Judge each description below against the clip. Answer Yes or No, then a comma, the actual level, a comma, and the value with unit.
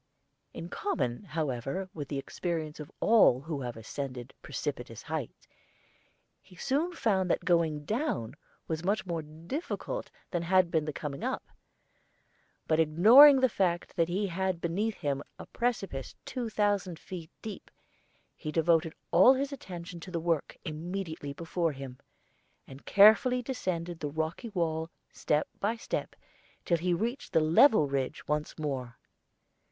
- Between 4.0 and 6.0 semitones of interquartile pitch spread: Yes, average, 5.0 semitones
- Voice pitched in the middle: Yes, medium, 170 Hz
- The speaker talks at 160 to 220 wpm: No, average, 145 wpm